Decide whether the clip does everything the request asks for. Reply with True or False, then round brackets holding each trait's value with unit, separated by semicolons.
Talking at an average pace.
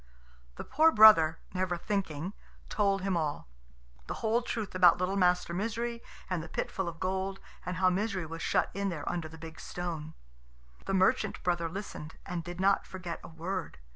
True (180 wpm)